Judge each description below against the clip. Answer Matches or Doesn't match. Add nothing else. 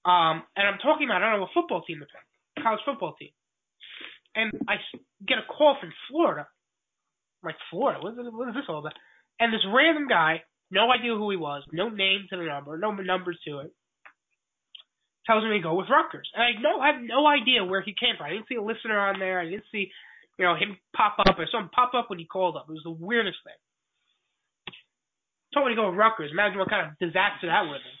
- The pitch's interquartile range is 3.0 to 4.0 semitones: Doesn't match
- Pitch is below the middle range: Doesn't match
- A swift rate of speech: Matches